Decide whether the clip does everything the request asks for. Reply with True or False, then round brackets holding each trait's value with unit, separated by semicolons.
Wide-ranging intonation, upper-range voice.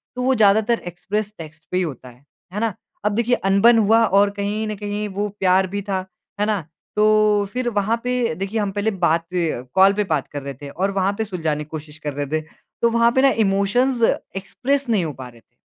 False (4.1 semitones; 200 Hz)